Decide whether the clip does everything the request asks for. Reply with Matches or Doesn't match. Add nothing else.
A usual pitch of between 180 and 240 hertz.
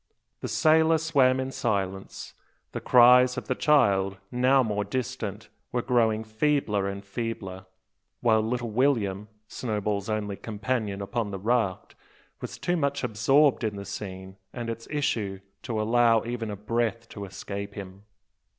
Doesn't match